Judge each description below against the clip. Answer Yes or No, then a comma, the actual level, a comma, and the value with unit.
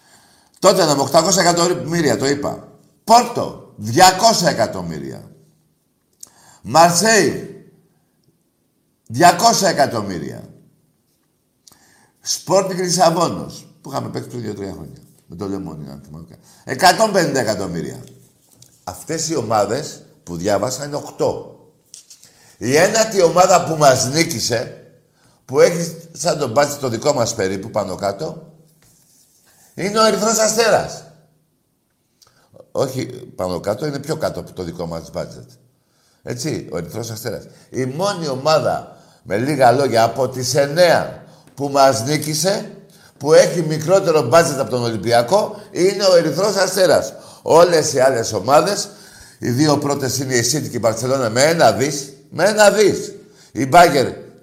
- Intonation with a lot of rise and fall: Yes, wide, 6.3 semitones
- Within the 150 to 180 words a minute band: No, average, 125 wpm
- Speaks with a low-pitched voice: No, medium, 160 Hz